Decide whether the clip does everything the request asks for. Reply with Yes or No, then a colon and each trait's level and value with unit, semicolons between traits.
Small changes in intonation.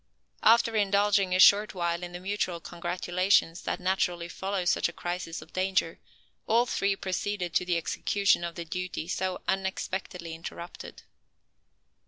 Yes: narrow, 2.2 semitones